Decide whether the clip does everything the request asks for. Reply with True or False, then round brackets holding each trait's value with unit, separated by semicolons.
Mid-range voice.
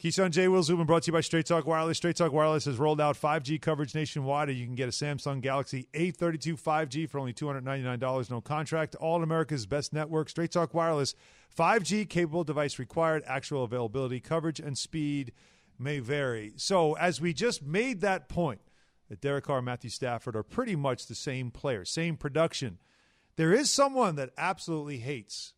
True (155 Hz)